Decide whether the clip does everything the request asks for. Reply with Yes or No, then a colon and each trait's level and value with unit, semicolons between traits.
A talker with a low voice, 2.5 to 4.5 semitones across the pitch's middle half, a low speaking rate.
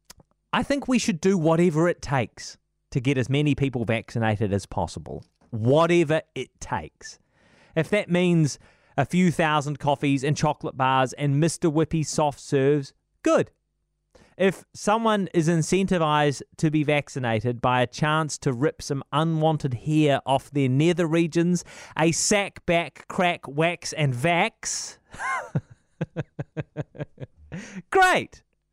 No: medium, 155 Hz; average, 3.8 semitones; slow, 130 wpm